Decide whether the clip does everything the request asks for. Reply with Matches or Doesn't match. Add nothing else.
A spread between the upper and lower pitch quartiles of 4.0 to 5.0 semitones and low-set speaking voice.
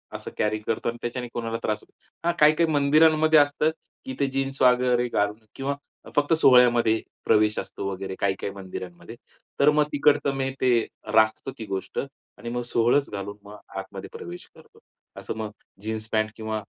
Matches